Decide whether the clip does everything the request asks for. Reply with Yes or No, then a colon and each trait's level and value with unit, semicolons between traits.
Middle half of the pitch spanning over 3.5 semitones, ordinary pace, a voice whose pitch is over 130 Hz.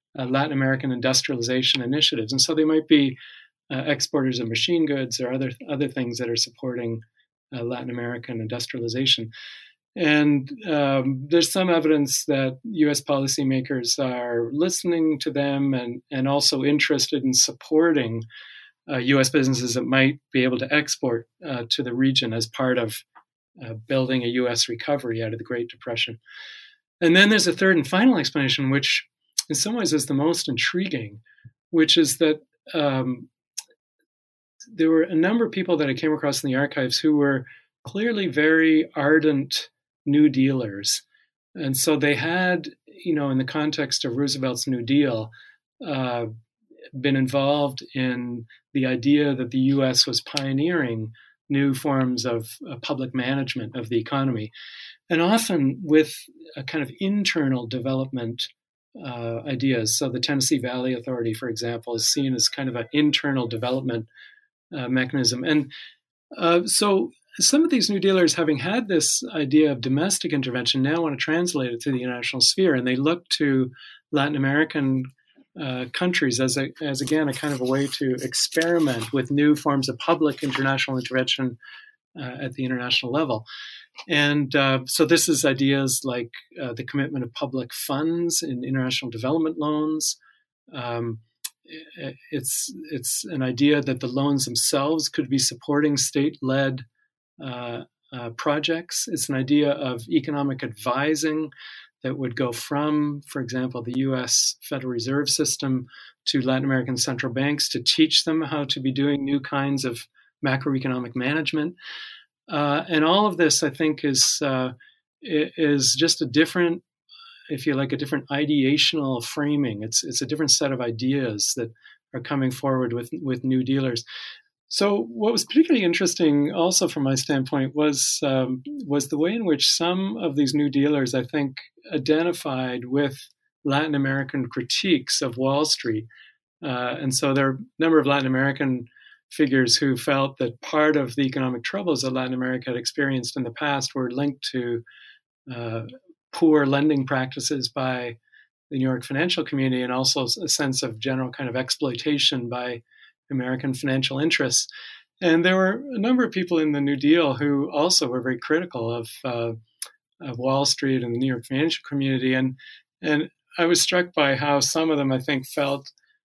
No: average, 3.2 semitones; average, 165 wpm; medium, 140 Hz